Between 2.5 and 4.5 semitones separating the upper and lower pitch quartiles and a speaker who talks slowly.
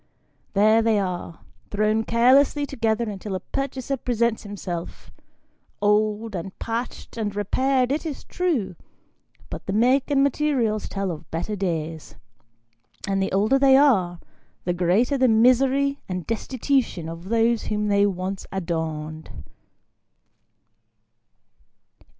No: average, 5.3 semitones; slow, 120 wpm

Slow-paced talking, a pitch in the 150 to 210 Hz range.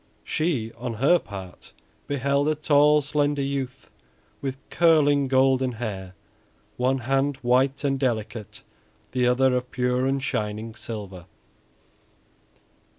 No: slow, 115 wpm; low, 130 Hz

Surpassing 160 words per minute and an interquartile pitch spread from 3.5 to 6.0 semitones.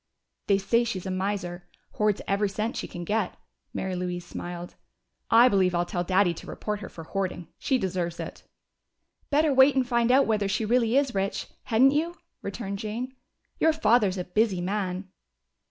Yes: average, 175 wpm; average, 4.5 semitones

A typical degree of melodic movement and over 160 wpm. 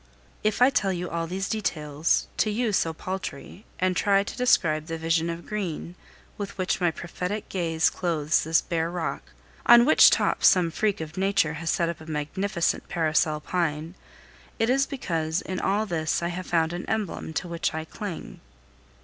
Yes: average, 3.5 semitones; average, 180 wpm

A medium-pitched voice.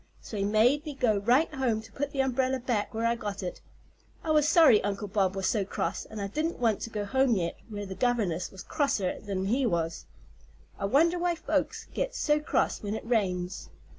No: high, 225 Hz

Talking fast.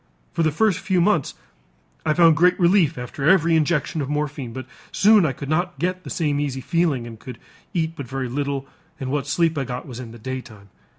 Yes: fast, 215 wpm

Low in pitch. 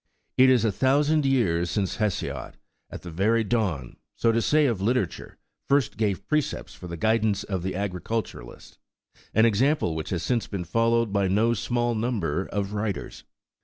Yes: low, 110 Hz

